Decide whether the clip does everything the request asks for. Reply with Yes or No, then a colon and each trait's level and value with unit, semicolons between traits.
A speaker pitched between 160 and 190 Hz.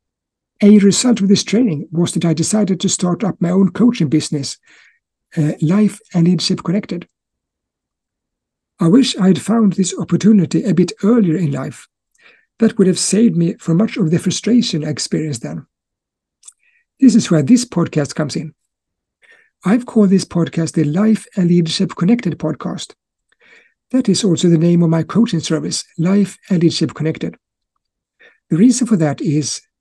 Yes: medium, 185 Hz